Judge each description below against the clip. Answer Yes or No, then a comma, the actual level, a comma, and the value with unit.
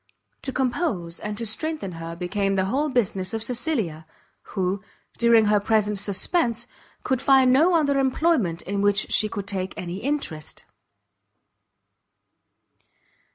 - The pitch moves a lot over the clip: Yes, wide, 5.8 semitones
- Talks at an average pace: No, slow, 130 wpm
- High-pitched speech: Yes, high, 210 Hz